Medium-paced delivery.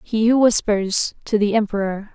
Yes: average, 170 wpm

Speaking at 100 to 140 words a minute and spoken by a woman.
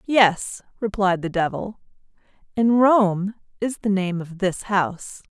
Yes: slow, 135 wpm; female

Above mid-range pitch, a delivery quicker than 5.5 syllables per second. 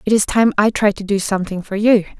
Yes: high, 205 Hz; 6.3 syllables/s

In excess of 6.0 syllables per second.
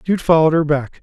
Yes: 6.5 syllables/s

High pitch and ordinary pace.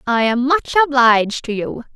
Yes: very high, 255 Hz; average, 185 wpm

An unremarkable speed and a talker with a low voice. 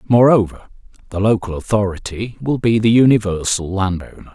No: slow, 125 wpm; low, 105 Hz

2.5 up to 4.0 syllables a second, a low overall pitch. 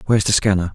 No: 8.3 syllables/s; very low, 95 Hz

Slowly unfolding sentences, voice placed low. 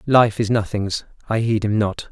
No: average, 200 wpm; low, 110 Hz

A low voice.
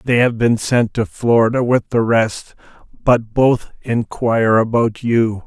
Yes: low, 115 Hz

